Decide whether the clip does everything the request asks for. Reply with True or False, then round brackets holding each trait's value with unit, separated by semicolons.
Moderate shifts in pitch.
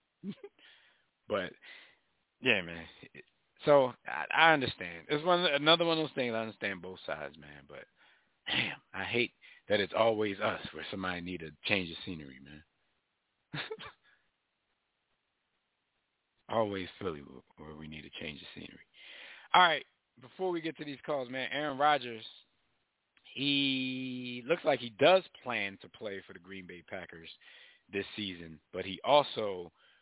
False (8.0 semitones)